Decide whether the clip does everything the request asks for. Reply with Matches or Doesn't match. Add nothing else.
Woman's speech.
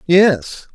Doesn't match